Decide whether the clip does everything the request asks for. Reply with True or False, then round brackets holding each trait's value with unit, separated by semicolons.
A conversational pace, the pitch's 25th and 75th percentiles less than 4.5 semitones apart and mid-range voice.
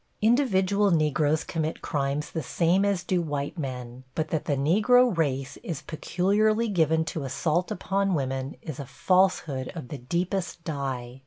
False (155 wpm; 5.2 semitones; 160 Hz)